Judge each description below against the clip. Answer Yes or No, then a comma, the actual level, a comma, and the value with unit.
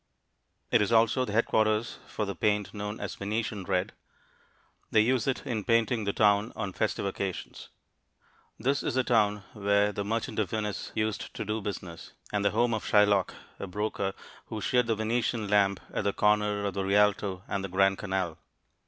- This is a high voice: No, low, 105 Hz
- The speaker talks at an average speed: Yes, average, 180 wpm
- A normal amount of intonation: No, narrow, 1.9 semitones